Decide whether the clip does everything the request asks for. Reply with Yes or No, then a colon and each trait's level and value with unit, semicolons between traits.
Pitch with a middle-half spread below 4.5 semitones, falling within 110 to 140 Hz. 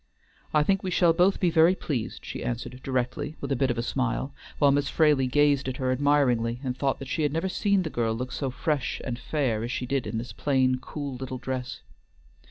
Yes: average, 2.9 semitones; low, 135 Hz